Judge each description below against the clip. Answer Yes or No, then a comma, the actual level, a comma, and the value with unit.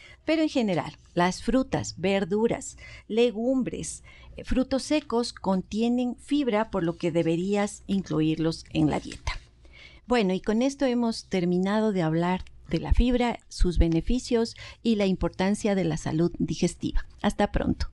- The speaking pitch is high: Yes, high, 200 Hz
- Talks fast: No, average, 135 wpm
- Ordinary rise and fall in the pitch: No, wide, 5.9 semitones